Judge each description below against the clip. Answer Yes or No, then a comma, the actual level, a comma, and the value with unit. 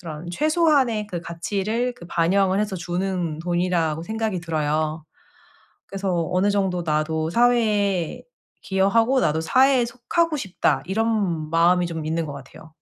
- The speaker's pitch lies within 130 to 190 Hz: Yes, medium, 185 Hz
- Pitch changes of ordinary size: Yes, average, 4.9 semitones